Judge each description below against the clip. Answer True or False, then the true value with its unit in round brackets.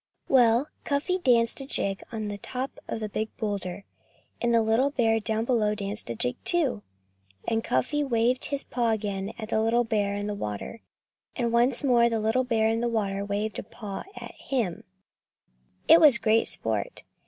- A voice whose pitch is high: True (225 Hz)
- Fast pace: False (185 wpm)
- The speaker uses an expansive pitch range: False (2.8 semitones)